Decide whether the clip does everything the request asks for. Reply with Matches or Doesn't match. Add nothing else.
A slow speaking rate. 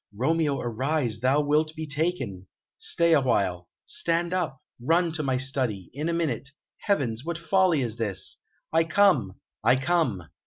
Doesn't match